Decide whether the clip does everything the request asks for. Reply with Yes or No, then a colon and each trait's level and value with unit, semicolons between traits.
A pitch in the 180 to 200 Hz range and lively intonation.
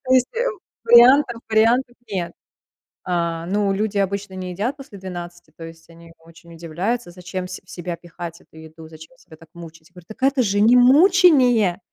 Yes: medium, 185 Hz; wide, 5.9 semitones